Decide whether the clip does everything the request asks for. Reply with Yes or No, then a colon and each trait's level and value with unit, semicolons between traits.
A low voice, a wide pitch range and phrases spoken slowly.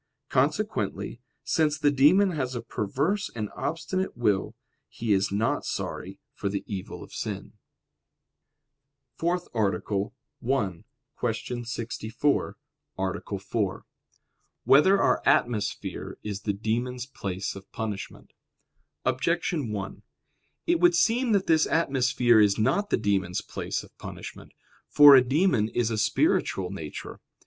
Yes: low, 120 Hz; wide, 6.6 semitones; slow, 125 wpm